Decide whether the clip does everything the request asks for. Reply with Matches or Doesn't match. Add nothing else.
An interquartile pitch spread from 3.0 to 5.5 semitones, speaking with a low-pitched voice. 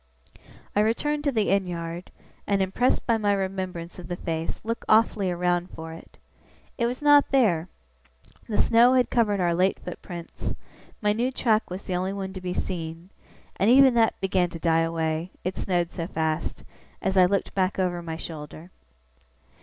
Doesn't match